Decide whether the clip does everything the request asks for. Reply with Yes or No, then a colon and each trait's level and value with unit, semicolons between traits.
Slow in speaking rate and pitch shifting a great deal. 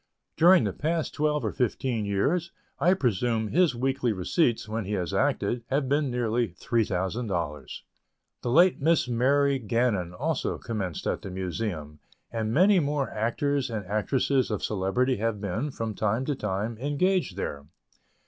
No: average, 150 wpm; wide, 5.7 semitones